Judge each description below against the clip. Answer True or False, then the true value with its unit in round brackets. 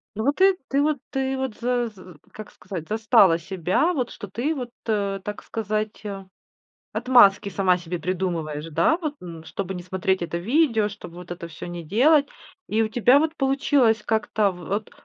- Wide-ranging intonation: True (5.7 semitones)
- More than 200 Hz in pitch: True (210 Hz)